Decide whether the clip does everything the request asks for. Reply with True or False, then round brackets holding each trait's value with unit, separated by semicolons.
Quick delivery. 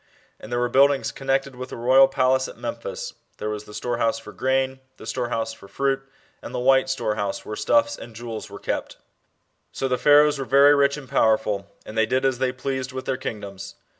True (210 wpm)